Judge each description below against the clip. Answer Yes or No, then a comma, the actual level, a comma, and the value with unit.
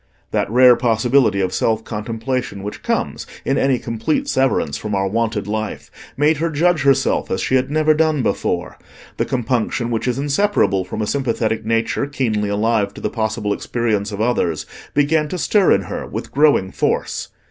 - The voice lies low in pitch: Yes, low, 115 Hz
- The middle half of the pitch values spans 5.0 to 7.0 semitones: No, average, 4.6 semitones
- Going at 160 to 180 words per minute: Yes, average, 175 wpm